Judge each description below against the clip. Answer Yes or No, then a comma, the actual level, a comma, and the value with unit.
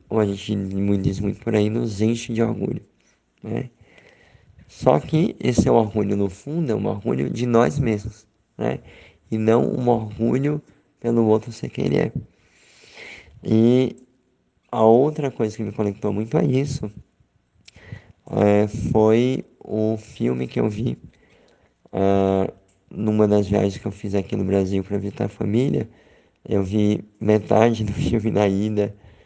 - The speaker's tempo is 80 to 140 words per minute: No, average, 150 wpm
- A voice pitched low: Yes, low, 110 Hz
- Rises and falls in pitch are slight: Yes, narrow, 2.3 semitones